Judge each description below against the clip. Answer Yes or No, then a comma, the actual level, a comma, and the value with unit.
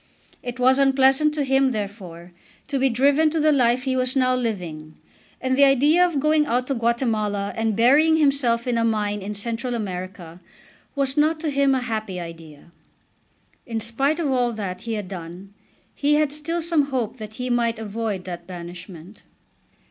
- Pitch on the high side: Yes, high, 240 Hz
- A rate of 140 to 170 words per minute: No, average, 180 wpm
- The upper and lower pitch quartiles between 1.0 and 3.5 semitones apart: No, average, 5.3 semitones